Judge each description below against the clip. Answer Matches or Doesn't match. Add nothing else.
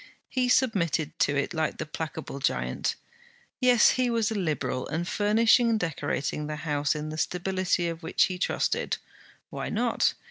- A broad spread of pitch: Matches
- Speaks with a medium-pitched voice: Matches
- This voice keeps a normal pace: Matches